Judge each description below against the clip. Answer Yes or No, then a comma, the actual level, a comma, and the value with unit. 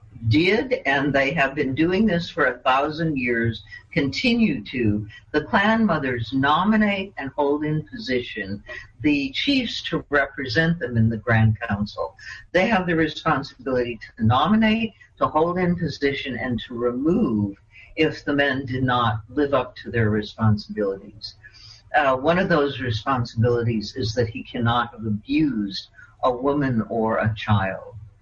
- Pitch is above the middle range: No, low, 130 Hz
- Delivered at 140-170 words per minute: Yes, average, 145 wpm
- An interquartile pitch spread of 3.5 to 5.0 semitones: No, wide, 5.6 semitones